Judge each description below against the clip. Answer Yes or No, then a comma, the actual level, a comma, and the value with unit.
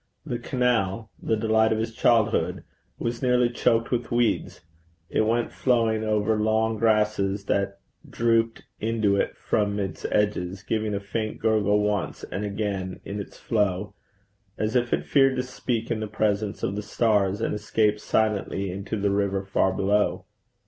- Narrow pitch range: Yes, narrow, 2.1 semitones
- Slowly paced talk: No, average, 160 wpm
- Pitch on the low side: Yes, low, 110 Hz